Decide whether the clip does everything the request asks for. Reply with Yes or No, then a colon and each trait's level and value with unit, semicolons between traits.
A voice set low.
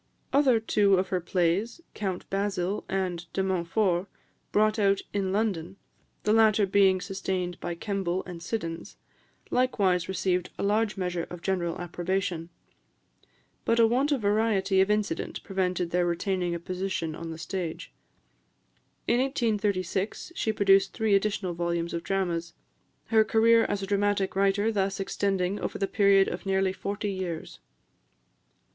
No: high, 195 Hz